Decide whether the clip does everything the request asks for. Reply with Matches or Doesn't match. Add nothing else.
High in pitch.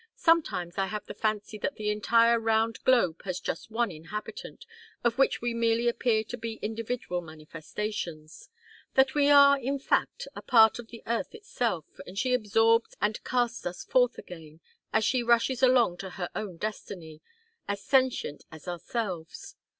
Matches